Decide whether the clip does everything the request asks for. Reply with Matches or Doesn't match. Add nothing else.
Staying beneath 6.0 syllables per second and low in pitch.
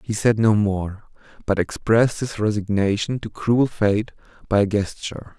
Matches